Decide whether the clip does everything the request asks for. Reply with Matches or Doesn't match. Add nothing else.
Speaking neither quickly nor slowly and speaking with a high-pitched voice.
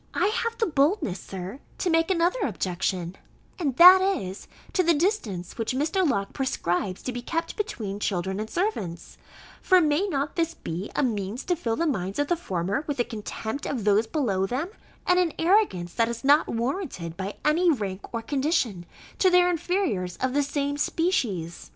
Matches